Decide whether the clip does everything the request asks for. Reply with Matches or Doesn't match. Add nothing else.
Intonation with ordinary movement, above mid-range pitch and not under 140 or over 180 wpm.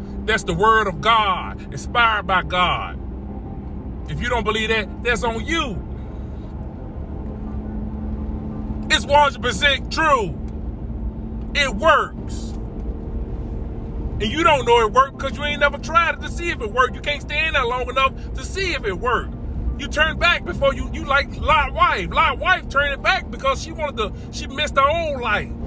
Doesn't match